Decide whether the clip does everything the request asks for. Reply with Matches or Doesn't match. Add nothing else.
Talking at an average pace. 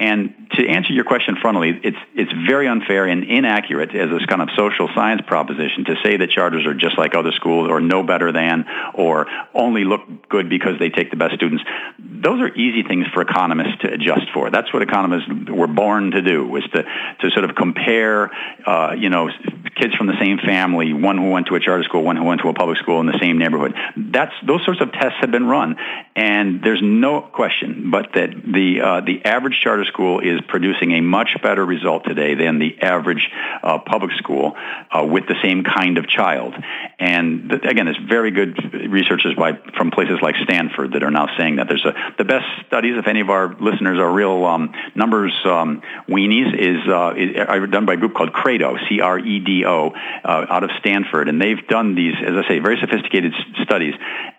Doesn't match